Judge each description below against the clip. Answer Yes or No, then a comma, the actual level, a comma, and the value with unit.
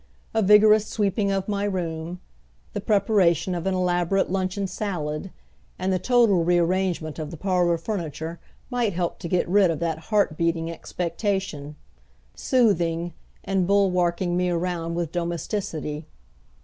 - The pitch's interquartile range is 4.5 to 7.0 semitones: No, average, 2.9 semitones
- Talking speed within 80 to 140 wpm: Yes, slow, 135 wpm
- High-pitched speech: No, medium, 180 Hz